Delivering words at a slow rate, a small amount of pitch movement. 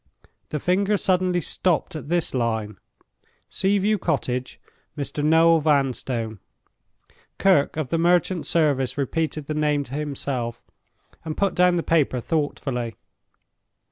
No: slow, 125 wpm; average, 4.7 semitones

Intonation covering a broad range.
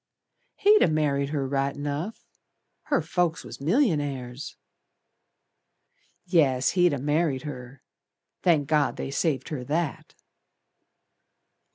No: average, 3.3 semitones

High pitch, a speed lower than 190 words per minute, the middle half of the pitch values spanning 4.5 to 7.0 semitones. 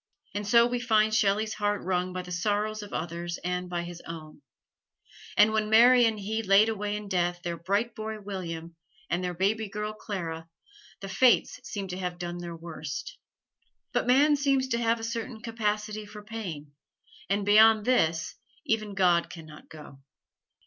No: high, 205 Hz; average, 175 wpm; average, 3.9 semitones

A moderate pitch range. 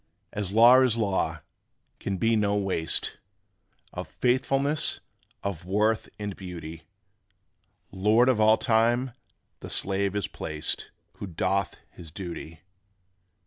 Yes: average, 3.5 semitones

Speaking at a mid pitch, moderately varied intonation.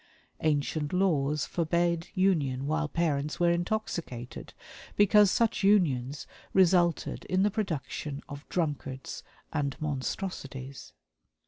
Yes: medium, 160 Hz; average, 4.6 semitones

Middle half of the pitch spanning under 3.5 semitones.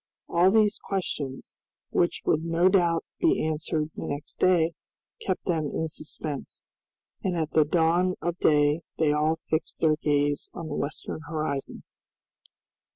Yes: narrow, 2.4 semitones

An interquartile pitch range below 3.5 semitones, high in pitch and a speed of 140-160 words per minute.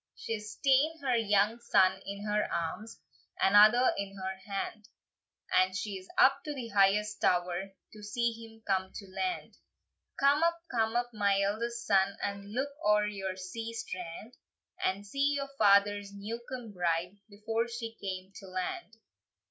Yes: average, 3.1 semitones; high, 210 Hz; average, 155 wpm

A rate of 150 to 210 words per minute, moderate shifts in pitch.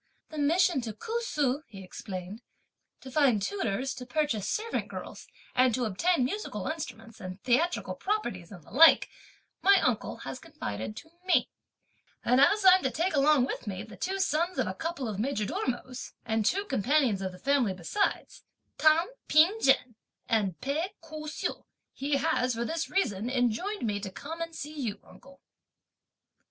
No: average, 165 wpm; wide, 6.9 semitones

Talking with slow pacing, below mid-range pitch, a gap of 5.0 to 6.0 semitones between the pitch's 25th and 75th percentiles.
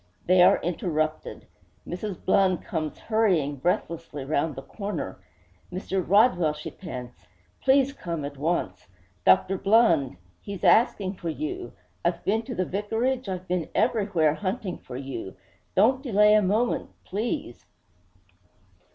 No: slow, 130 wpm; medium, 185 Hz; wide, 5.4 semitones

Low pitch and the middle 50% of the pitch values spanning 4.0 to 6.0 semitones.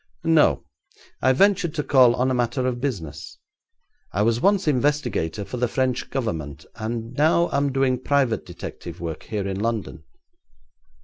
Yes: low, 125 Hz; average, 4.5 semitones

